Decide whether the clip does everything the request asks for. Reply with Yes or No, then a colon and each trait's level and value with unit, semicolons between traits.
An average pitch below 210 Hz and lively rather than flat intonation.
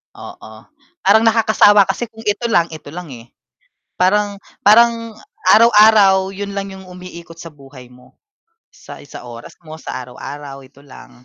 Yes: medium, 185 Hz; wide, 6.6 semitones